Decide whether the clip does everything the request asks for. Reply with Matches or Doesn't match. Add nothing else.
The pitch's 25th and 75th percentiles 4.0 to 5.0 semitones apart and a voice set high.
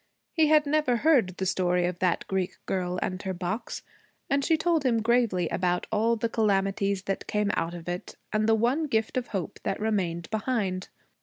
Matches